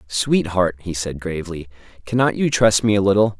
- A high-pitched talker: No, low, 100 Hz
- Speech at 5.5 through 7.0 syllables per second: No, 5.3 syllables/s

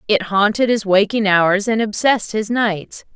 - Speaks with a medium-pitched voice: No, high, 210 Hz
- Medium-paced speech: Yes, average, 170 wpm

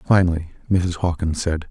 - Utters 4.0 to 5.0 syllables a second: No, 5.2 syllables/s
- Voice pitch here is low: Yes, very low, 85 Hz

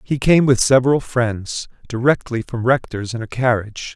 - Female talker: No, male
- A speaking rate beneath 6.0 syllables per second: Yes, 4.9 syllables/s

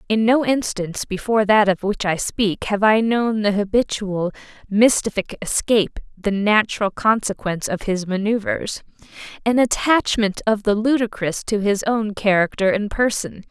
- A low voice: No, high, 210 Hz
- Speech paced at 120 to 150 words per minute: Yes, average, 140 wpm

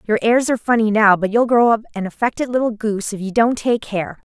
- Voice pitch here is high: Yes, high, 220 Hz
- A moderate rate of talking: No, fast, 250 wpm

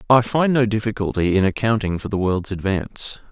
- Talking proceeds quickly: No, average, 180 wpm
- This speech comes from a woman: No, male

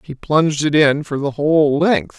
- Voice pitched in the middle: Yes, medium, 145 Hz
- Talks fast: Yes, fast, 220 wpm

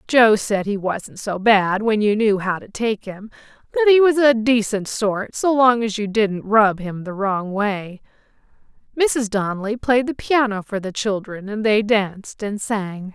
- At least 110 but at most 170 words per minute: No, average, 190 wpm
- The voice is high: Yes, high, 215 Hz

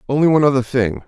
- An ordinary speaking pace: No, fast, 225 wpm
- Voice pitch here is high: No, low, 135 Hz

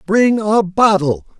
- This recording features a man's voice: Yes, male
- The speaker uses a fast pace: No, slow, 130 wpm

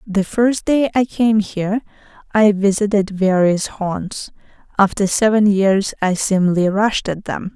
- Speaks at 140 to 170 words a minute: Yes, average, 145 wpm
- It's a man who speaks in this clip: No, female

